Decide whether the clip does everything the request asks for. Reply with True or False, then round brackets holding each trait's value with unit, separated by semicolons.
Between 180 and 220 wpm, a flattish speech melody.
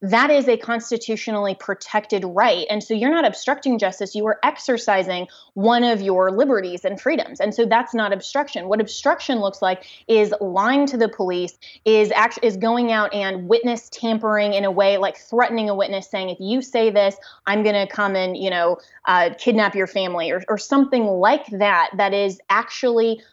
False (190 wpm; 3.0 semitones)